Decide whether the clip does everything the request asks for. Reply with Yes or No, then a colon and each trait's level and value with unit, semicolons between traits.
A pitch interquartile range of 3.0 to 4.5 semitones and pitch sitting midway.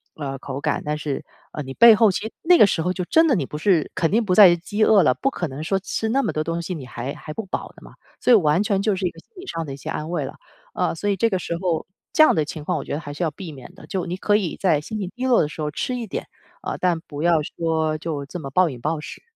No: average, 4.9 semitones; medium, 170 Hz